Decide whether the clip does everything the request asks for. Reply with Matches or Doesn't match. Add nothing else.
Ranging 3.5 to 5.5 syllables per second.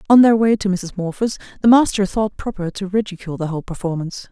Doesn't match